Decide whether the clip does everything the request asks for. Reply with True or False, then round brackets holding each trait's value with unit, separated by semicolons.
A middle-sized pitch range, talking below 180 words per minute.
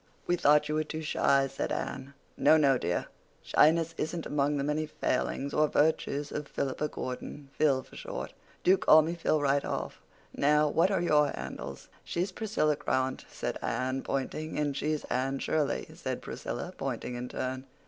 False (2.3 semitones; 160 wpm)